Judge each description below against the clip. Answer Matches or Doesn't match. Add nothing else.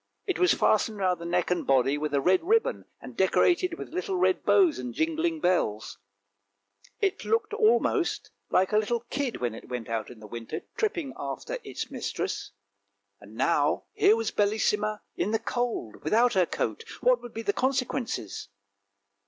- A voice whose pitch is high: Matches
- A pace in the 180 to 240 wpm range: Doesn't match